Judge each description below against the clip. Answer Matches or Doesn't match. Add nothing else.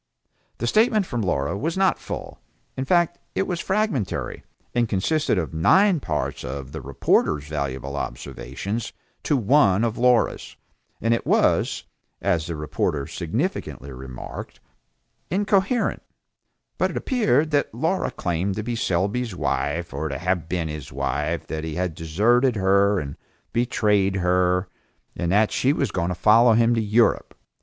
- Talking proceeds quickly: Doesn't match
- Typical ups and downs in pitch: Doesn't match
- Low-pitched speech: Matches